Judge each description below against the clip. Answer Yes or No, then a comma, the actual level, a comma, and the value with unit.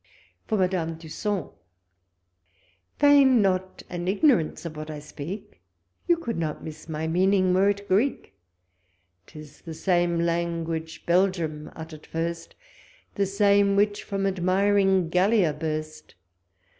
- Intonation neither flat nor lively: Yes, average, 3.7 semitones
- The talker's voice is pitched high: No, medium, 180 Hz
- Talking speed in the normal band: No, slow, 125 wpm